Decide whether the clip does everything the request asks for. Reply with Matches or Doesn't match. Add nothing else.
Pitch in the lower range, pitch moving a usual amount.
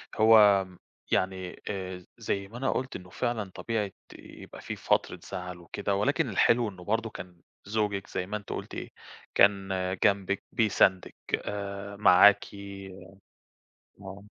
Doesn't match